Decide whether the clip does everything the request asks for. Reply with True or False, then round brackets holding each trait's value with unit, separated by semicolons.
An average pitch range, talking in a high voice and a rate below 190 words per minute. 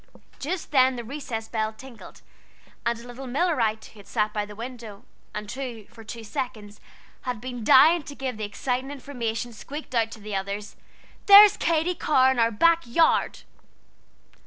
True (3.8 semitones; 240 Hz; 165 wpm)